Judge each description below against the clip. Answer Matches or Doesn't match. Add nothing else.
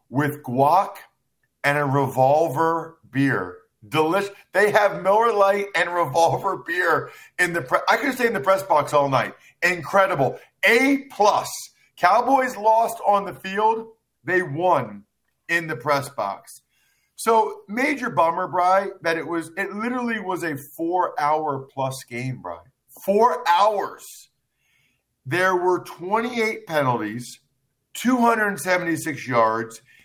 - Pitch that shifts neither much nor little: Doesn't match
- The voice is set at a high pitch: Doesn't match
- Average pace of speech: Doesn't match